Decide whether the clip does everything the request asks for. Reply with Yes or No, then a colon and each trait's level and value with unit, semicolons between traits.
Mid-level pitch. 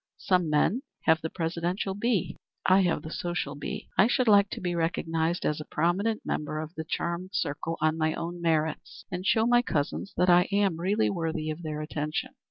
Yes: medium, 170 Hz